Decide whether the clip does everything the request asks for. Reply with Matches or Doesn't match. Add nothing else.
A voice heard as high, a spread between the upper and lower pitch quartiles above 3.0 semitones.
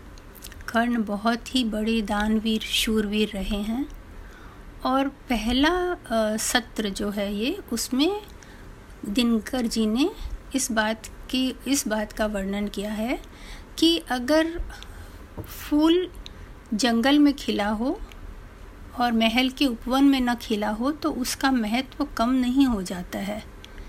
Matches